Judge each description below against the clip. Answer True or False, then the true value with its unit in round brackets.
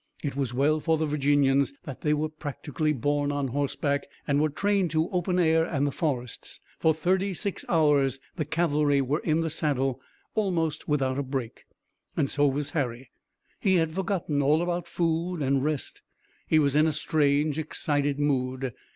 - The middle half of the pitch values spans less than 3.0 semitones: True (2.5 semitones)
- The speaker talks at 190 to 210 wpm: False (175 wpm)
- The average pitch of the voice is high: False (150 Hz)